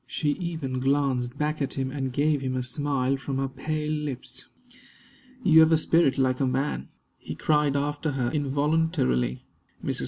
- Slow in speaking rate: No, average, 165 wpm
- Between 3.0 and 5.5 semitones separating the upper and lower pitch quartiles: No, narrow, 2.6 semitones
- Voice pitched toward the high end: No, medium, 140 Hz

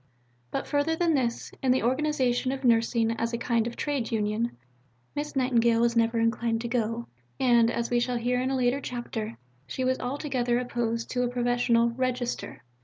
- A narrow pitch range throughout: Yes, narrow, 1.7 semitones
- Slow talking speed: No, average, 180 wpm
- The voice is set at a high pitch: Yes, high, 240 Hz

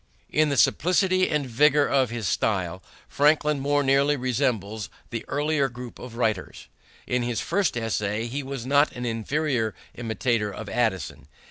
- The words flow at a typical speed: Yes, average, 150 wpm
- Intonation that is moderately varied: Yes, average, 4.4 semitones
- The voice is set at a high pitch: No, low, 125 Hz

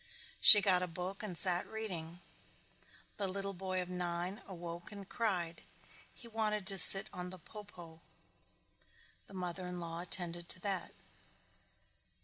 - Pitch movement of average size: No, narrow, 2.2 semitones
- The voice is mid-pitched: Yes, medium, 180 Hz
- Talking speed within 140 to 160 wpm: Yes, average, 145 wpm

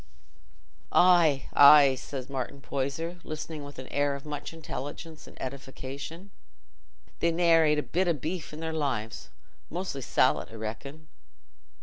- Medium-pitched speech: Yes, medium, 145 Hz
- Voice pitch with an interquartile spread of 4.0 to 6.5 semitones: No, average, 3.0 semitones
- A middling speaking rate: Yes, average, 145 wpm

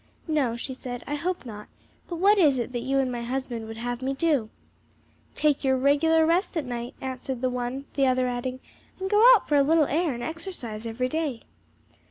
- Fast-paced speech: Yes, fast, 210 wpm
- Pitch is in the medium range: No, very high, 265 Hz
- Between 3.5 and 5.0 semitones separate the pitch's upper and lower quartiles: Yes, average, 4.3 semitones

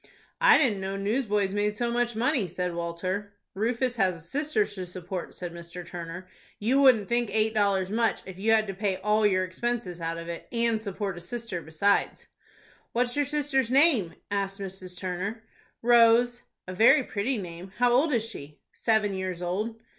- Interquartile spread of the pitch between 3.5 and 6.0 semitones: Yes, average, 4.3 semitones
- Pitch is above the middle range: Yes, high, 205 Hz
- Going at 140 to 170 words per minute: No, average, 185 wpm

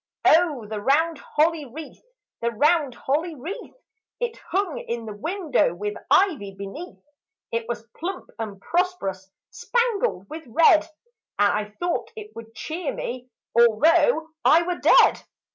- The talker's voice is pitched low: No, very high, 305 Hz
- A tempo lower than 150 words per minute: Yes, average, 140 wpm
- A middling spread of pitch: No, wide, 7.5 semitones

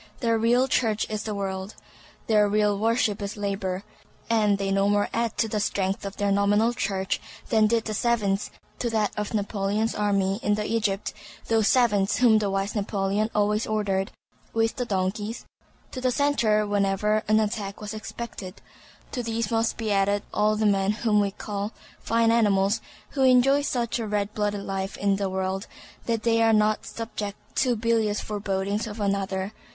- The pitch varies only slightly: Yes, narrow, 2.1 semitones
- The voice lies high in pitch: Yes, high, 210 Hz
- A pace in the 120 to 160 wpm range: No, average, 170 wpm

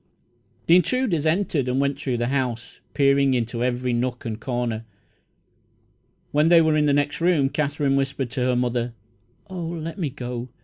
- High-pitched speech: No, low, 135 Hz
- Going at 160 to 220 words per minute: Yes, average, 170 wpm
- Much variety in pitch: No, average, 3.9 semitones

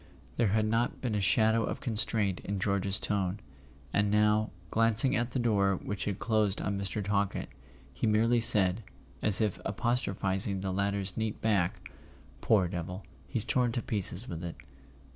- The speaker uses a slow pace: No, average, 160 wpm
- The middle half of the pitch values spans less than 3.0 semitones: Yes, narrow, 2.5 semitones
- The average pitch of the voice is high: No, low, 105 Hz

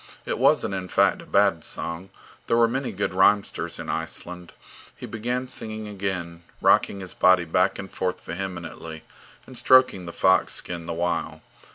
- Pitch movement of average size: Yes, average, 3.7 semitones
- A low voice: Yes, very low, 95 Hz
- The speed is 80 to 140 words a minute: No, average, 165 wpm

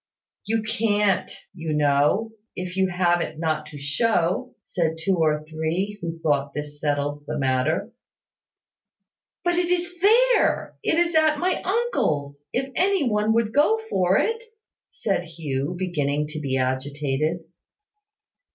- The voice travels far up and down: Yes, wide, 7.5 semitones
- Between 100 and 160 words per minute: Yes, average, 140 wpm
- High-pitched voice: No, medium, 175 Hz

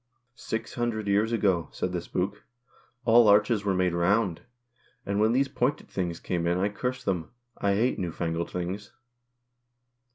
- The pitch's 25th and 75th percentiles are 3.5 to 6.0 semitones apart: Yes, average, 4.0 semitones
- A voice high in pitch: No, low, 100 Hz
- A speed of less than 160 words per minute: No, average, 165 wpm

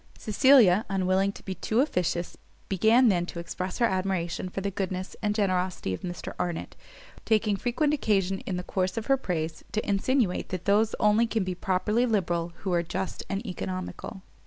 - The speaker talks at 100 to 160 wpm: No, average, 180 wpm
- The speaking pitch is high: Yes, high, 195 Hz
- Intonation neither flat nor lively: Yes, average, 3.2 semitones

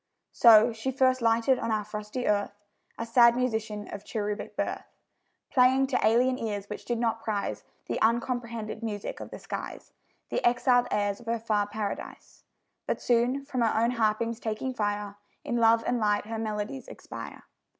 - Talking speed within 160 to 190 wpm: Yes, average, 170 wpm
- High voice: Yes, high, 230 Hz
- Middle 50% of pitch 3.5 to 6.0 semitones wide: No, narrow, 2.5 semitones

